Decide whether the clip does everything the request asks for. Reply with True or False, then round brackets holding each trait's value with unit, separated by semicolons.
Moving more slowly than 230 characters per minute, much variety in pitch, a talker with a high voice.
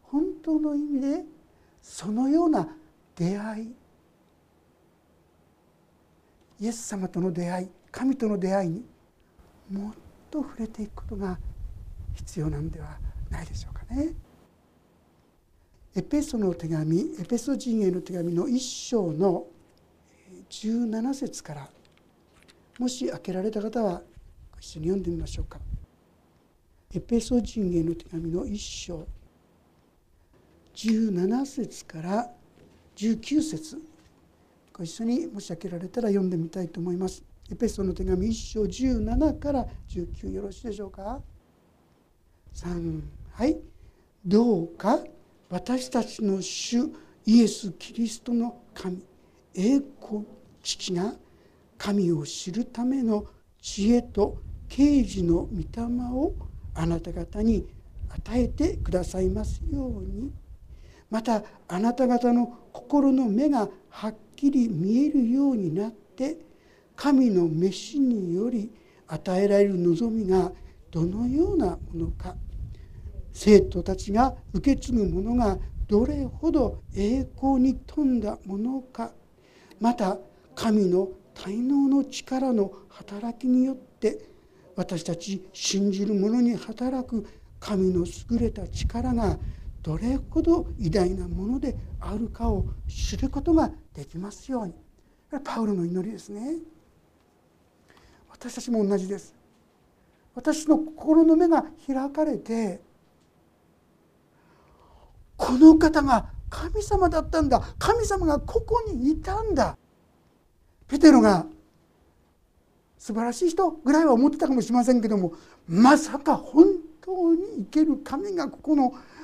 True (215 characters per minute; 6.5 semitones; 220 Hz)